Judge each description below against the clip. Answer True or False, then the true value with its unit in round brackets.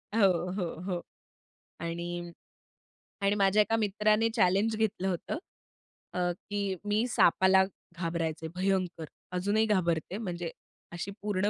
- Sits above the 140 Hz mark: True (190 Hz)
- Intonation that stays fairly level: False (3.2 semitones)